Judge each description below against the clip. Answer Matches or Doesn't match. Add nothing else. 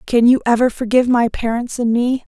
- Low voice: Doesn't match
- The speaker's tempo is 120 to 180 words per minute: Doesn't match